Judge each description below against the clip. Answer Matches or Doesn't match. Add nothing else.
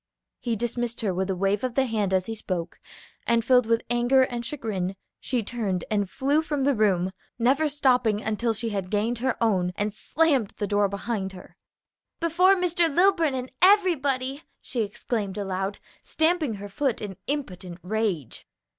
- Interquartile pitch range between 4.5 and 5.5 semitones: Matches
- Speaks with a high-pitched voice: Matches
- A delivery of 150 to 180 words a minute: Matches